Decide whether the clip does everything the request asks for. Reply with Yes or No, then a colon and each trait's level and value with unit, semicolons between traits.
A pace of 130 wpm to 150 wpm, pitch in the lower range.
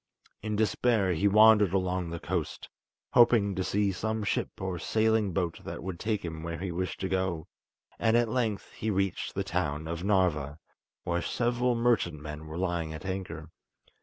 No: average, 170 wpm; very low, 95 Hz